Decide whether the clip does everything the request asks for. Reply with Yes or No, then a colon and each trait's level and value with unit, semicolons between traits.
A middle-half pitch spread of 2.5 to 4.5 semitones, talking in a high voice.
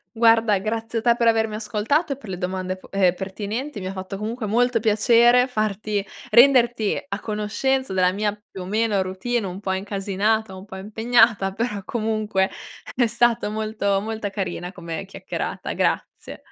Yes: average, 2.8 semitones; high, 215 Hz